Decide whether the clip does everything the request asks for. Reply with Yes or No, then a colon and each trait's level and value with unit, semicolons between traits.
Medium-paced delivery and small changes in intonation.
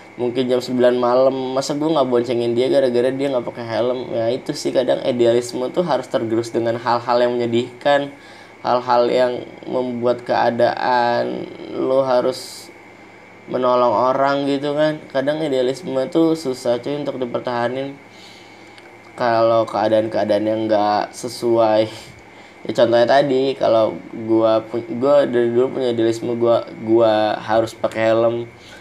Yes: average, 130 wpm; narrow, 2.3 semitones